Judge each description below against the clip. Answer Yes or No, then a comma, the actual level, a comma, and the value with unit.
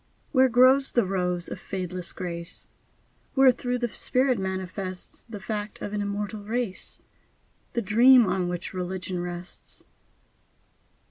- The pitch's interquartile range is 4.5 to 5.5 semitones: Yes, average, 4.8 semitones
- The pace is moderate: No, slow, 125 wpm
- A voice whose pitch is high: Yes, high, 200 Hz